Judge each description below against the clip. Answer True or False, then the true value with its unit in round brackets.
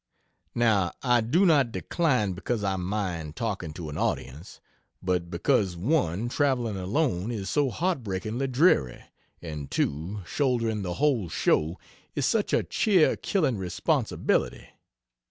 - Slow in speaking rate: True (130 wpm)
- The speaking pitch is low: True (105 Hz)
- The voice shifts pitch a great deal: True (6.8 semitones)